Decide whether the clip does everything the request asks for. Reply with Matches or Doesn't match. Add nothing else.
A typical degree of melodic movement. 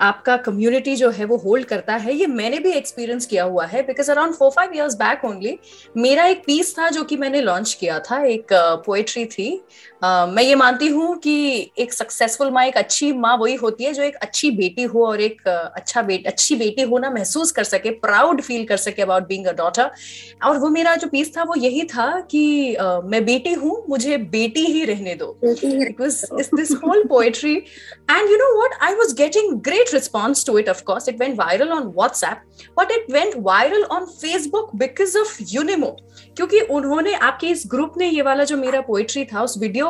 Doesn't match